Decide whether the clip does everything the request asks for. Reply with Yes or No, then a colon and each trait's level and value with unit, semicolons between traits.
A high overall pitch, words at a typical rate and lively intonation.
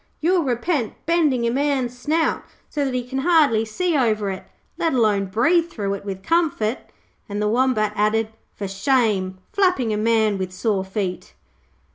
Yes: high, 235 Hz; average, 165 wpm; wide, 5.7 semitones